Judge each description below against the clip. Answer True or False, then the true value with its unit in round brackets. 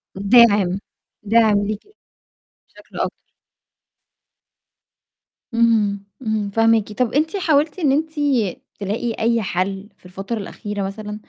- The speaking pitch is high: True (215 Hz)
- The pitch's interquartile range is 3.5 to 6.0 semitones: False (2.7 semitones)